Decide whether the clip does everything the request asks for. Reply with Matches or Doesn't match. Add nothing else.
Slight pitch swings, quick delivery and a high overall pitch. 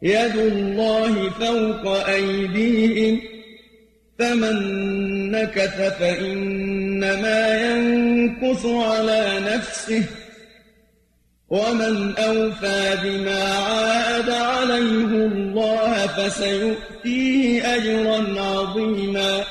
Doesn't match